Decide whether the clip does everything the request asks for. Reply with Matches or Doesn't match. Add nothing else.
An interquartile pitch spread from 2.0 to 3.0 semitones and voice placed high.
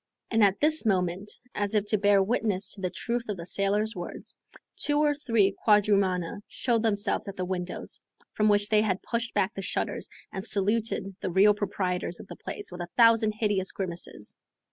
Matches